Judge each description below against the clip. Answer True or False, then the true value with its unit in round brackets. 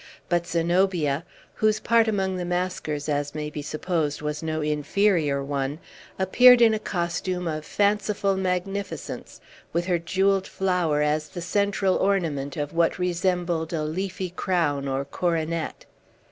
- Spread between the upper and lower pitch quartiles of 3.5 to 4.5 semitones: True (4.0 semitones)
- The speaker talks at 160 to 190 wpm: False (140 wpm)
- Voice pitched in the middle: True (175 Hz)